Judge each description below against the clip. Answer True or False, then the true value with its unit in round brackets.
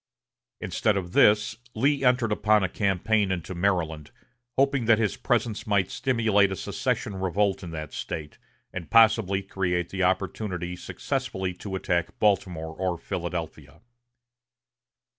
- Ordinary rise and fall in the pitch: True (3.6 semitones)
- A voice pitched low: True (95 Hz)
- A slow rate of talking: True (130 wpm)